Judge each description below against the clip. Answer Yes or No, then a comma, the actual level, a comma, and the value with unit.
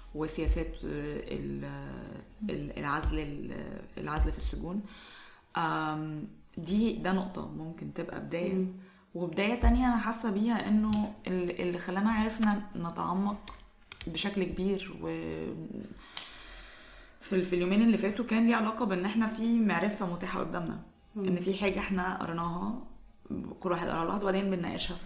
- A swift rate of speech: No, average, 115 wpm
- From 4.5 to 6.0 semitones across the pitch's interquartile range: No, average, 4.0 semitones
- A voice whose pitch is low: No, medium, 185 Hz